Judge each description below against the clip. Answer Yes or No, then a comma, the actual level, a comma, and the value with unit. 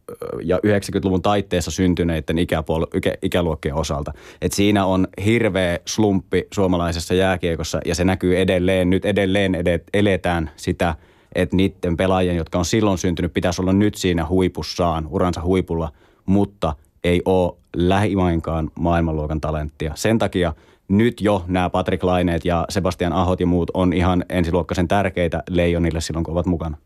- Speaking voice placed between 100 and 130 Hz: No, very low, 90 Hz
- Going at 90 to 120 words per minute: No, average, 145 wpm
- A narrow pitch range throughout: Yes, narrow, 1.9 semitones